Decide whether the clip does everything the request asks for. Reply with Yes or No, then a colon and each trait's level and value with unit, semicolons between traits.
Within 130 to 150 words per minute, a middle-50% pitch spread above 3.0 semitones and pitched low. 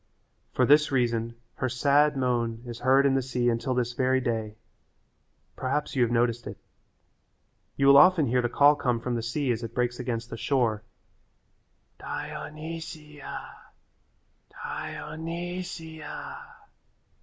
Yes: average, 145 wpm; average, 3.7 semitones; low, 130 Hz